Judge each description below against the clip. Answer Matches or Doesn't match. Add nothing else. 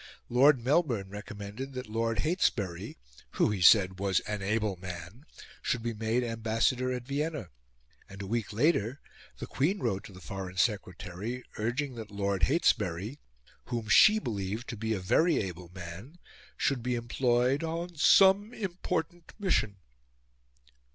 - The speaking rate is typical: Matches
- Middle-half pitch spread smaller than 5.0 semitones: Doesn't match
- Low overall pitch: Matches